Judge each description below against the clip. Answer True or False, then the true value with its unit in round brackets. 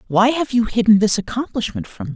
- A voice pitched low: False (210 Hz)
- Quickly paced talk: True (225 wpm)